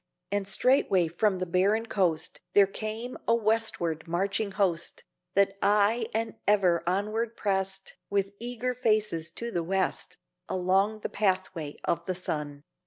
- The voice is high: Yes, high, 195 Hz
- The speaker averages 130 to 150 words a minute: Yes, average, 140 wpm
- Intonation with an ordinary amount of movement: Yes, average, 3.2 semitones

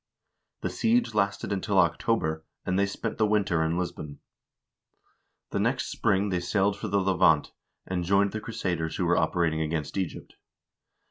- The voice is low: Yes, very low, 95 Hz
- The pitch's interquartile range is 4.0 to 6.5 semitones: No, average, 3.5 semitones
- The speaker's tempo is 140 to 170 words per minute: Yes, average, 155 wpm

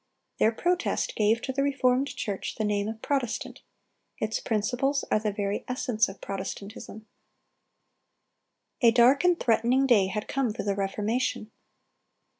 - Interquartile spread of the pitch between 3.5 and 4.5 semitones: Yes, average, 3.9 semitones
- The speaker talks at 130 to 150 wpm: Yes, average, 140 wpm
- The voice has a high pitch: Yes, high, 225 Hz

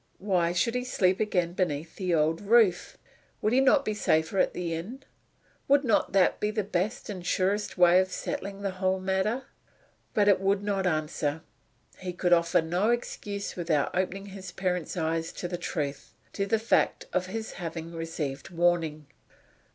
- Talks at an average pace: Yes, average, 175 wpm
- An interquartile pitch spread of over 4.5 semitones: No, average, 3.2 semitones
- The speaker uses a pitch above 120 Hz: Yes, medium, 185 Hz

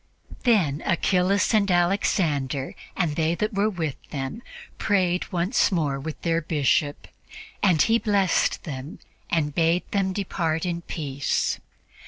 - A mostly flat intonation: No, average, 4.5 semitones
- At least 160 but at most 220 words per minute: No, slow, 135 wpm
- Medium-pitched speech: Yes, medium, 170 Hz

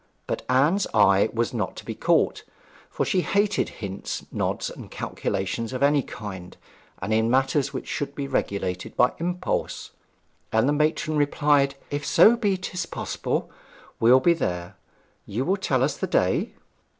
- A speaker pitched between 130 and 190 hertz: Yes, low, 135 Hz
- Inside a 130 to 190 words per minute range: Yes, average, 155 wpm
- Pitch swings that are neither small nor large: No, wide, 5.7 semitones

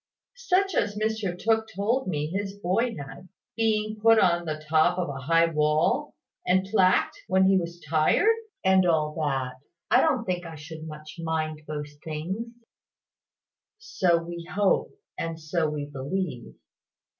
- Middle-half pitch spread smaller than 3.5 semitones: No, average, 4.9 semitones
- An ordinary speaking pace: Yes, average, 150 wpm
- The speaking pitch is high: No, medium, 175 Hz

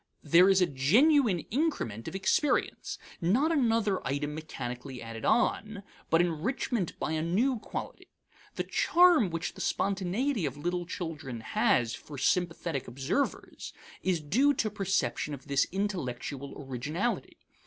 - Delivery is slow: Yes, slow, 130 wpm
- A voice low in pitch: No, medium, 175 Hz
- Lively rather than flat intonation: Yes, wide, 7.3 semitones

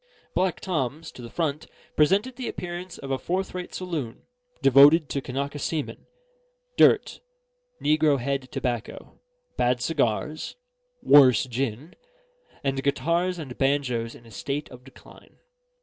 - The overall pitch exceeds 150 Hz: No, medium, 140 Hz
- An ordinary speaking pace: No, slow, 125 wpm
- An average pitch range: Yes, average, 4.5 semitones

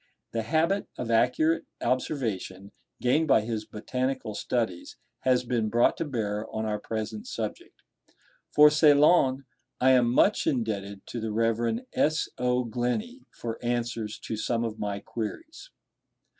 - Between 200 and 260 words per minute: No, average, 140 wpm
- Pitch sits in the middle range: No, low, 120 Hz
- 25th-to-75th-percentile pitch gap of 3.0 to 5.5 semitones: Yes, average, 3.7 semitones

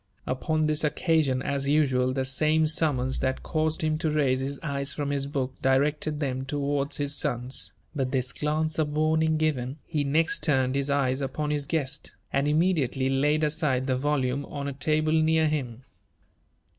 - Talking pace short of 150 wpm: No, average, 170 wpm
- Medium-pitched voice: Yes, medium, 145 Hz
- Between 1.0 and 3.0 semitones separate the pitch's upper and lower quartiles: Yes, narrow, 2.6 semitones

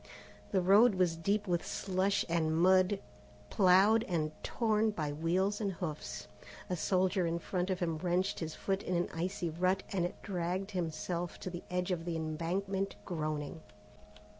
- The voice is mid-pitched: Yes, medium, 180 Hz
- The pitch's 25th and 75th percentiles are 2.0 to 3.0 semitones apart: Yes, narrow, 2.5 semitones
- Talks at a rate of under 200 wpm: Yes, average, 160 wpm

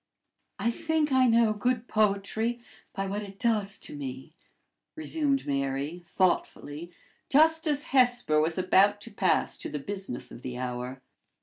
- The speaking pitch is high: Yes, high, 200 Hz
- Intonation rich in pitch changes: Yes, wide, 8.3 semitones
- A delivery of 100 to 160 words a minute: Yes, average, 145 wpm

